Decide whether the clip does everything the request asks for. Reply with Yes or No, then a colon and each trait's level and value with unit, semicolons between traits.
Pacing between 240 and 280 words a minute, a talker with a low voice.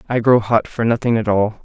Yes: fast, 255 wpm; low, 110 Hz